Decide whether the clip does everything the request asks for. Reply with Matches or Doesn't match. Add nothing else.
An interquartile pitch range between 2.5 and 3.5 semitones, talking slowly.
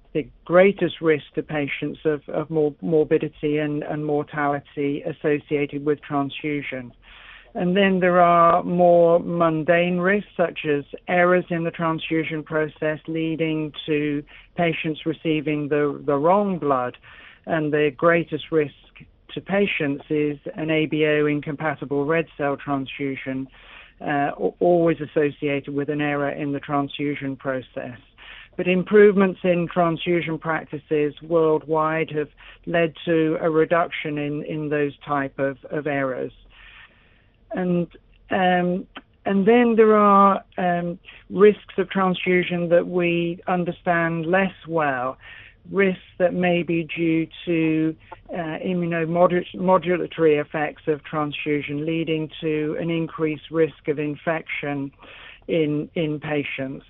Matches